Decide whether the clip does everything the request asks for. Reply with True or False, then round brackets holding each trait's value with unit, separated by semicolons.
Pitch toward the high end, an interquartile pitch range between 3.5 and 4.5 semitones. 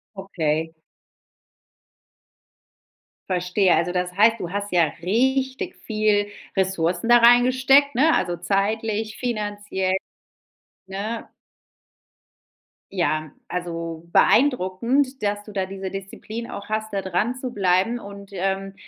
True (200 Hz; 4.0 semitones)